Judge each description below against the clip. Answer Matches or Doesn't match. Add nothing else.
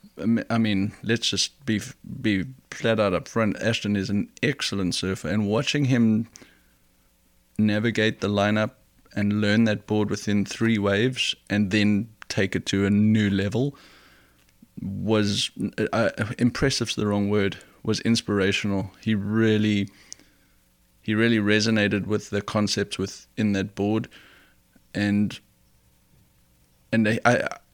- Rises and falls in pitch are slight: Matches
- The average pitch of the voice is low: Matches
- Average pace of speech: Doesn't match